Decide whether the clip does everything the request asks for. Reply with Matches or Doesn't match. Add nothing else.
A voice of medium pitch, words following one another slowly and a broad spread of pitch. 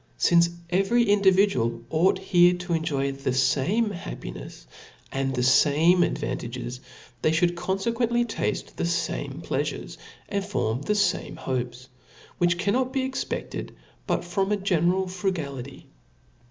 Matches